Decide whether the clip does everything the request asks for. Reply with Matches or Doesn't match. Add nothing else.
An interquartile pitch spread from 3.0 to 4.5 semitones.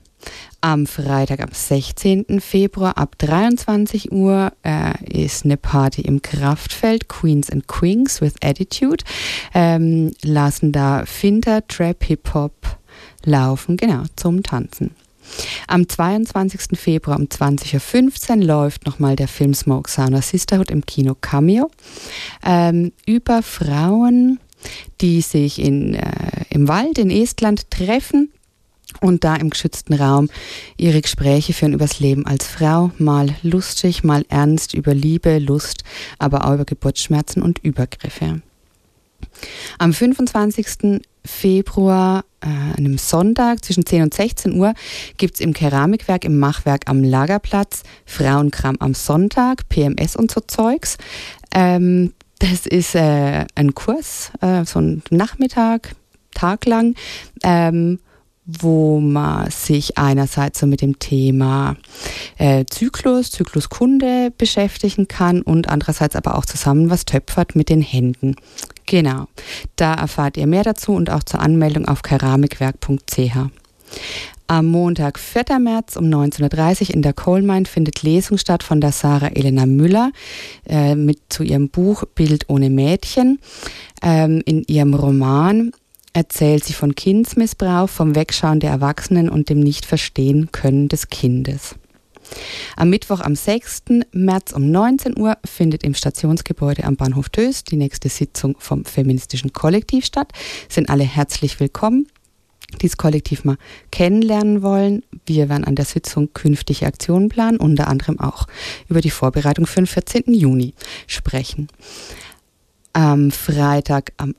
Doesn't match